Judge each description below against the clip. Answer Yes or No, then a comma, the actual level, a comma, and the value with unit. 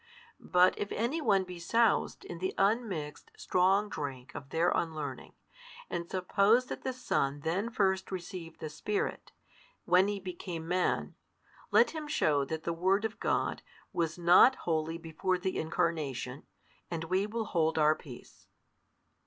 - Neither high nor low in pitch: Yes, medium, 180 Hz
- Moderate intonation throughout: Yes, average, 3.9 semitones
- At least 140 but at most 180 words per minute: Yes, average, 150 wpm